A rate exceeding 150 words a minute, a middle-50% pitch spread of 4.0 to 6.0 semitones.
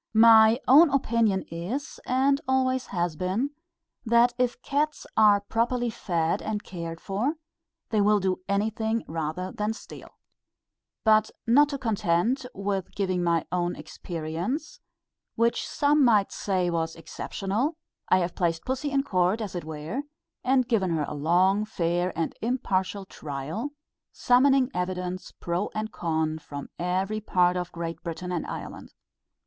No: average, 140 wpm; wide, 5.5 semitones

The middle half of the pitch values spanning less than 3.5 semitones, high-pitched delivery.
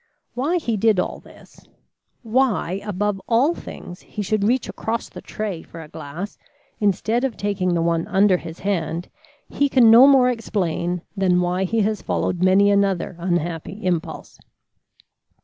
No: average, 4.0 semitones; high, 200 Hz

